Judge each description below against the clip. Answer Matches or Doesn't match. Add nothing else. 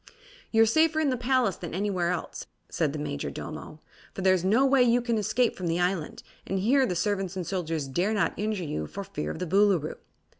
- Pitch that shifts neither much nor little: Matches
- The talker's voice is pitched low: Doesn't match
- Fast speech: Matches